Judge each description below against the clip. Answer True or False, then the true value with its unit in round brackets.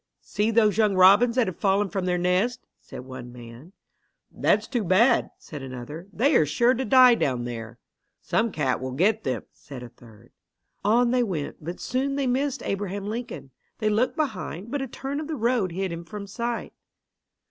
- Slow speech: False (190 wpm)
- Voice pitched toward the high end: True (200 Hz)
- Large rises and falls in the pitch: True (7.8 semitones)